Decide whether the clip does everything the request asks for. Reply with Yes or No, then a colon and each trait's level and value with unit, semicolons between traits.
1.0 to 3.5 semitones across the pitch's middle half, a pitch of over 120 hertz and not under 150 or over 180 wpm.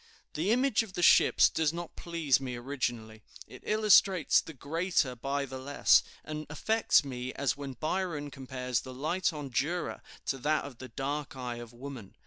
No: average, 4.5 semitones; medium, 140 Hz; average, 175 wpm